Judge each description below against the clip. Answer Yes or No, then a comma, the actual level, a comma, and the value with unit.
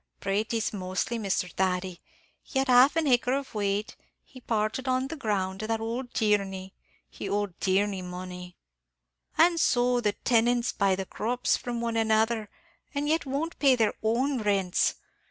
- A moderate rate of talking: Yes, average, 160 wpm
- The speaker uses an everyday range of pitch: Yes, average, 4.2 semitones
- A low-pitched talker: No, high, 220 Hz